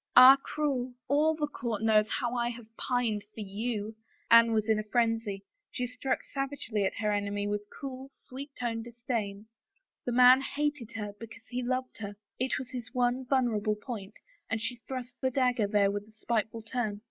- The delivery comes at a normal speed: Yes, average, 190 wpm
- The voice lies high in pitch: Yes, high, 235 Hz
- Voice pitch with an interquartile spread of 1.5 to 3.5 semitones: Yes, average, 3.1 semitones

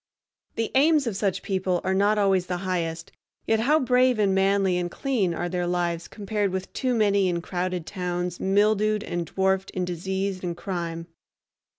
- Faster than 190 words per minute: No, average, 175 wpm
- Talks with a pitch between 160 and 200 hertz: Yes, high, 190 Hz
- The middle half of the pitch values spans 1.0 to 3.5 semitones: Yes, average, 2.9 semitones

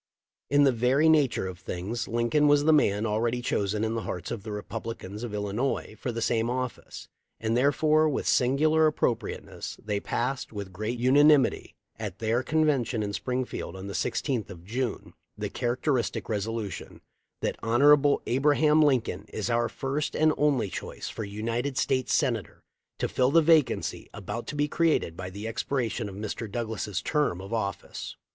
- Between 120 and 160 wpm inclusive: No, average, 170 wpm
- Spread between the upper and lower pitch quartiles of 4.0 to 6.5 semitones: Yes, average, 5.0 semitones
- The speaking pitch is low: Yes, low, 120 Hz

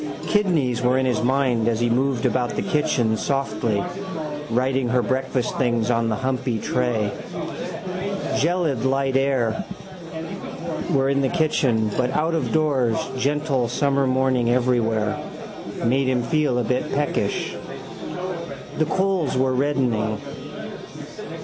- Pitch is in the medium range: No, low, 130 Hz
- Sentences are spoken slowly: Yes, slow, 130 wpm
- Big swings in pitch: No, average, 2.7 semitones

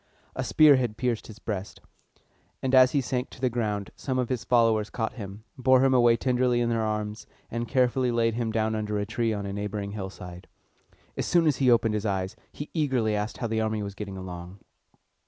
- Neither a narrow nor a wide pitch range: Yes, average, 3.2 semitones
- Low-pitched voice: Yes, low, 115 Hz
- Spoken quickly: Yes, fast, 210 wpm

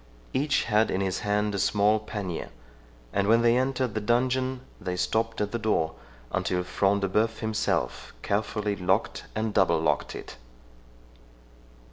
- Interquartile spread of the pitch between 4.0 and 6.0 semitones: No, average, 2.7 semitones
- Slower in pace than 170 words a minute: Yes, average, 150 wpm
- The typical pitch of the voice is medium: No, low, 105 Hz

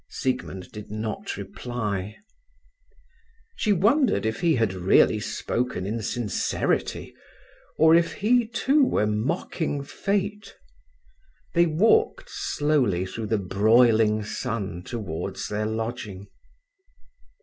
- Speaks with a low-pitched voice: Yes, low, 115 Hz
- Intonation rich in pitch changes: Yes, wide, 7.9 semitones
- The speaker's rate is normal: No, slow, 105 wpm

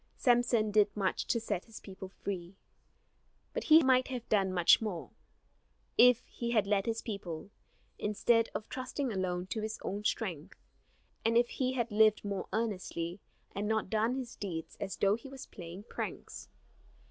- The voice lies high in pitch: Yes, high, 215 Hz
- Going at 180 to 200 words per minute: No, average, 165 wpm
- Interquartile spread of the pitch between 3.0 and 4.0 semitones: Yes, average, 3.6 semitones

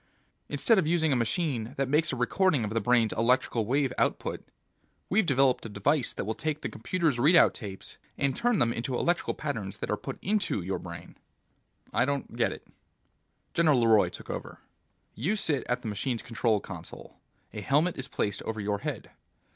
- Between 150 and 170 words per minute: No, average, 185 wpm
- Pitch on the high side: No, low, 125 Hz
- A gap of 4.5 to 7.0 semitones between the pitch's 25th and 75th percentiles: Yes, wide, 5.4 semitones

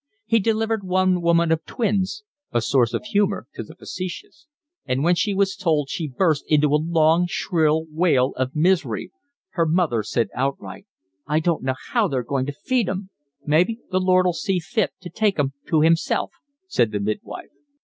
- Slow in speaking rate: No, average, 180 wpm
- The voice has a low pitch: No, medium, 170 Hz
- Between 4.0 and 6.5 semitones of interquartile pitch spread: Yes, average, 4.6 semitones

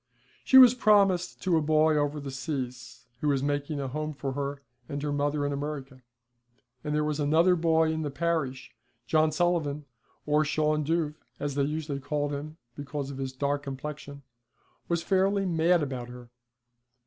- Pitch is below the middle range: No, medium, 150 Hz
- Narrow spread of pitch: Yes, narrow, 2.2 semitones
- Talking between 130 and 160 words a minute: No, average, 170 wpm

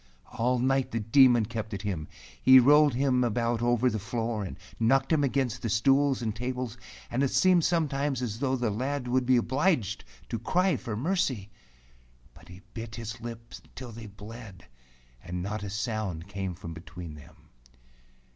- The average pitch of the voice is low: Yes, low, 120 Hz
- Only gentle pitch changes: No, average, 3.8 semitones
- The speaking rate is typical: Yes, average, 175 wpm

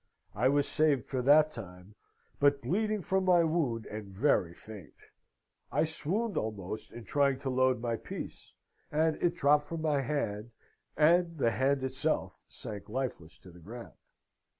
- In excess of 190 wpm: No, average, 155 wpm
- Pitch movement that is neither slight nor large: No, wide, 6.0 semitones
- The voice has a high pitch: No, low, 135 Hz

